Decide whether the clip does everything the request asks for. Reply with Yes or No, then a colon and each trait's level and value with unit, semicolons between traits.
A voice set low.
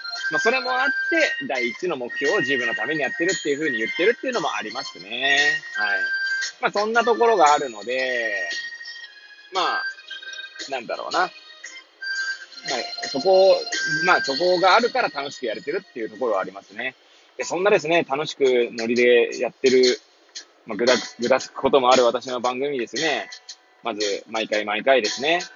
No: very high, 260 Hz